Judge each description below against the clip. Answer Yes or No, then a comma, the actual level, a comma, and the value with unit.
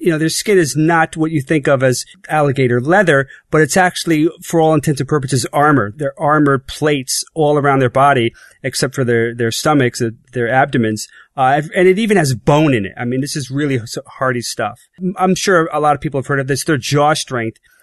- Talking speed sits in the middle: No, fast, 215 wpm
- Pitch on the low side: No, medium, 145 Hz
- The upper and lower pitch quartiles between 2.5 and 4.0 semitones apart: Yes, average, 3.4 semitones